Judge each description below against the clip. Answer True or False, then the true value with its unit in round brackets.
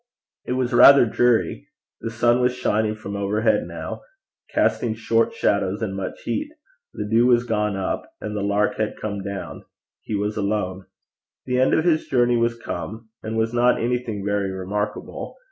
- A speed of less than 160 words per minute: False (170 wpm)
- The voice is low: True (110 Hz)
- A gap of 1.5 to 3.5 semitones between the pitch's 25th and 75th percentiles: True (2.9 semitones)